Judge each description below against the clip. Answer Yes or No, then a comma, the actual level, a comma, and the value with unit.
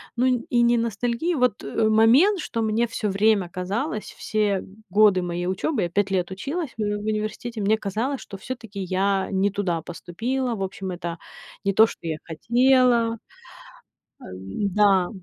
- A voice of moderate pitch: No, high, 210 Hz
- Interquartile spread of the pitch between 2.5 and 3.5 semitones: No, average, 3.9 semitones